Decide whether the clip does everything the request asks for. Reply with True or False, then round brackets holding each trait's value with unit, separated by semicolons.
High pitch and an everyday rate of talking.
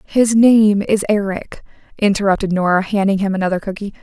True (200 Hz; 150 wpm)